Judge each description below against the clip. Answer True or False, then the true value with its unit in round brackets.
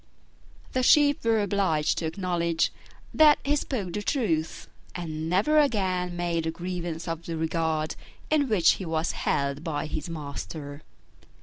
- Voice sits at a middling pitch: True (170 Hz)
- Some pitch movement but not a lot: True (4.3 semitones)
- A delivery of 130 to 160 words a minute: True (145 wpm)